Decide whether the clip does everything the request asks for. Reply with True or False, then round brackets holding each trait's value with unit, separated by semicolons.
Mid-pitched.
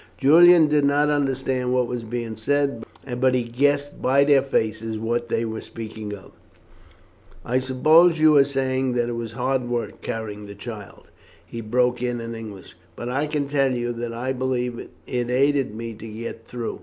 False (125 Hz)